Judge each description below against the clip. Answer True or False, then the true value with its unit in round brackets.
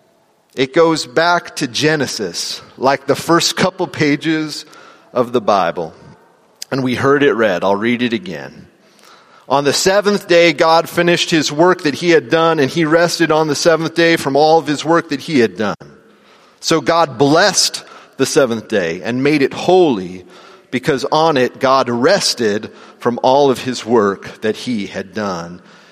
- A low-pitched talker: False (155 Hz)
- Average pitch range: True (4.1 semitones)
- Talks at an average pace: True (170 wpm)